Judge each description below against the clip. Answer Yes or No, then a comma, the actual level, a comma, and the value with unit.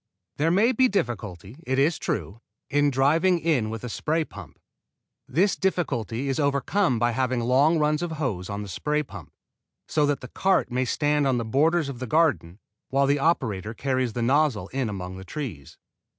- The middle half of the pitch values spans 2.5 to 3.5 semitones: No, average, 5.3 semitones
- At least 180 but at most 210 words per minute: Yes, average, 185 wpm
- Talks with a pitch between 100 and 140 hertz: Yes, low, 135 Hz